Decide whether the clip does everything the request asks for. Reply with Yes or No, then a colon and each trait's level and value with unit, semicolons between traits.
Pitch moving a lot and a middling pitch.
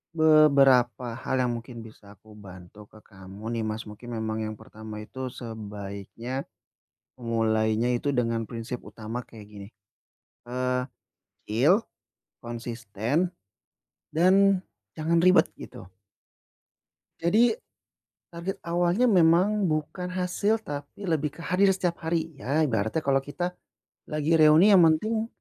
No: wide, 7.2 semitones; low, 130 Hz